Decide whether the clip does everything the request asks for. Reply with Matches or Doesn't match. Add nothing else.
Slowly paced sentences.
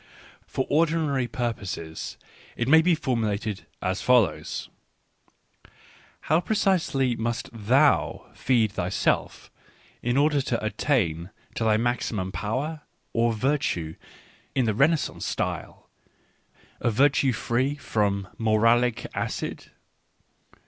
Matches